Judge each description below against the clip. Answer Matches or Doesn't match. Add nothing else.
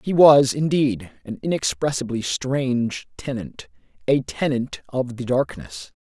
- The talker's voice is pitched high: Doesn't match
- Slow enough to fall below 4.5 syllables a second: Matches